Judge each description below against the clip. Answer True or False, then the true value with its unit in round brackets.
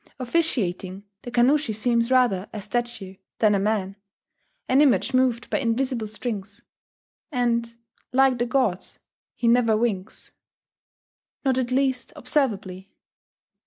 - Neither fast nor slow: False (120 wpm)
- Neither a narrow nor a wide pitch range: True (3.6 semitones)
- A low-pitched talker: False (235 Hz)